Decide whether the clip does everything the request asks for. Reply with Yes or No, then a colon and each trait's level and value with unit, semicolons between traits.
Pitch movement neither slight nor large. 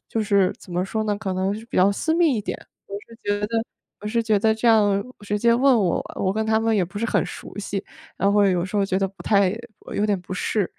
No: narrow, 2.2 semitones